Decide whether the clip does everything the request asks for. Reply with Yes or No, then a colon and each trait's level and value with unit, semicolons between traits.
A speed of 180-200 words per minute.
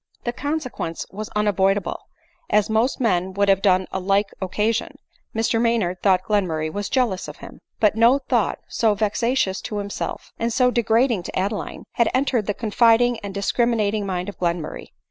Yes: average, 190 wpm